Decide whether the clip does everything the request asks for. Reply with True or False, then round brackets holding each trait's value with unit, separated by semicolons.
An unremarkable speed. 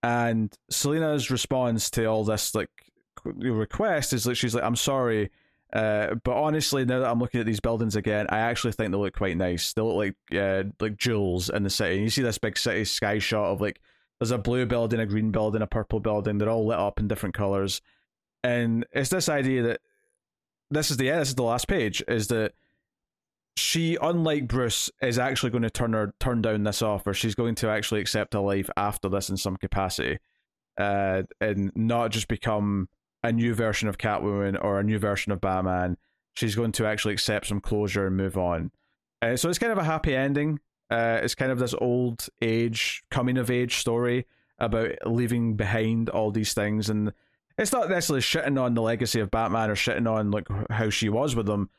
False (210 wpm)